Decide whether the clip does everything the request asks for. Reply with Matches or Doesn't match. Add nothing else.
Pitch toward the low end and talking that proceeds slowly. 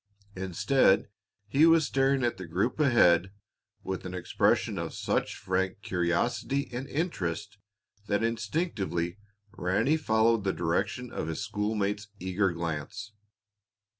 Matches